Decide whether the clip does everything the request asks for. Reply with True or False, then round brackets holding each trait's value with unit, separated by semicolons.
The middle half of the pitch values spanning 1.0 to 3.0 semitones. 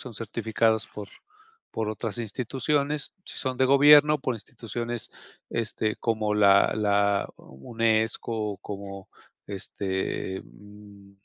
True (2.7 semitones)